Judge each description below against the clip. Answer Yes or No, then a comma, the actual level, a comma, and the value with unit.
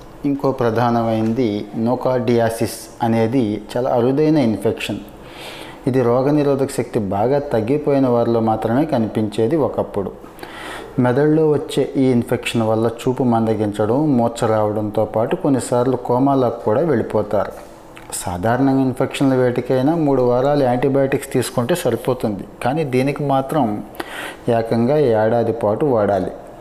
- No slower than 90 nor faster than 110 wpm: Yes, average, 100 wpm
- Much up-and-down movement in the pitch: No, average, 3.1 semitones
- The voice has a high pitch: No, low, 125 Hz